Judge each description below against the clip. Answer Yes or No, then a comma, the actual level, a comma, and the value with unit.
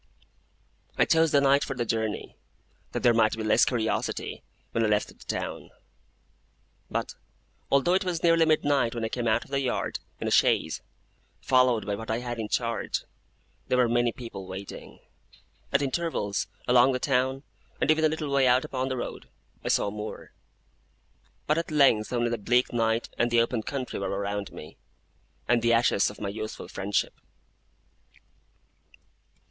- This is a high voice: No, low, 120 Hz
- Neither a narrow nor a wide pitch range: Yes, average, 3.6 semitones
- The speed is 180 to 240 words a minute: No, average, 170 wpm